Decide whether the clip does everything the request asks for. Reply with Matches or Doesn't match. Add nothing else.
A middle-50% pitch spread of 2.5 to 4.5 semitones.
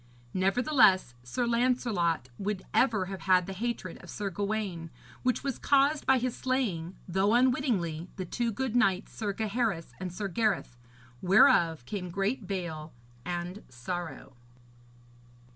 Doesn't match